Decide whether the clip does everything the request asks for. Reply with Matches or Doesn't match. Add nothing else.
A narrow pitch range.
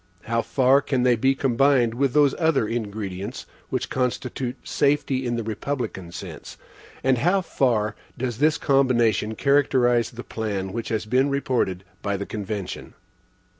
Doesn't match